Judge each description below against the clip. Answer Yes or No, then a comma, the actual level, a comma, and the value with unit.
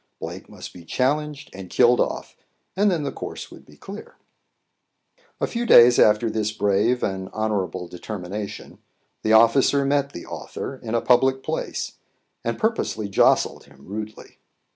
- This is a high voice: No, low, 110 Hz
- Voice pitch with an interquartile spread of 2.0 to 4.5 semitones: No, average, 5.0 semitones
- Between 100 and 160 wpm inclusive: Yes, average, 150 wpm